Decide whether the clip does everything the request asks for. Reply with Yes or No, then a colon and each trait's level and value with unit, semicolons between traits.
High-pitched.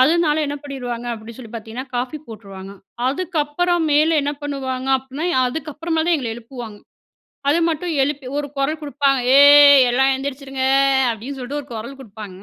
Yes: very high, 275 Hz